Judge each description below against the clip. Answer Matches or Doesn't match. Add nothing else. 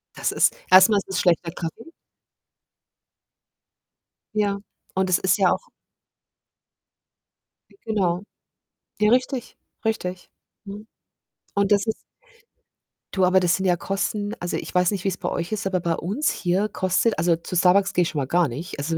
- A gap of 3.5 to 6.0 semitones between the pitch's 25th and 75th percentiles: Doesn't match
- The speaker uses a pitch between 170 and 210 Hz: Matches